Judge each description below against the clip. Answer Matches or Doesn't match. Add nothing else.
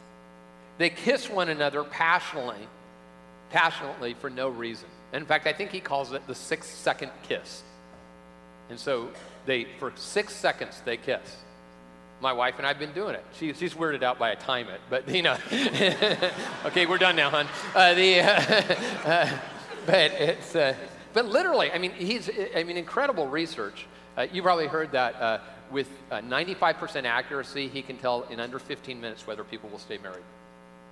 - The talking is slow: Doesn't match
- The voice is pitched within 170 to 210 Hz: Doesn't match